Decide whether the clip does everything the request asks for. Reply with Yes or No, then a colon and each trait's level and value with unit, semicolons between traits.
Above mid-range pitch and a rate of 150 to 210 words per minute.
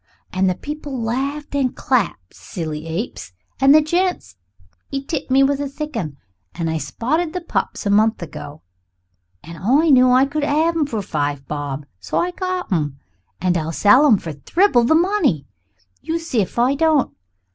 Yes: very high, 255 Hz; average, 180 wpm